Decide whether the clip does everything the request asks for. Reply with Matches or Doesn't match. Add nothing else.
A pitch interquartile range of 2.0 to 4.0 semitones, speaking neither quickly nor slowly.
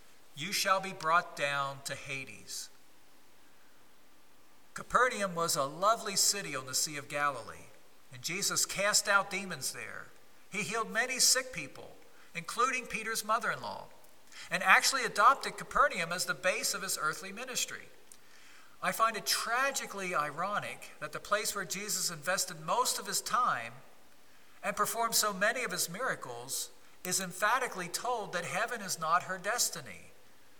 Doesn't match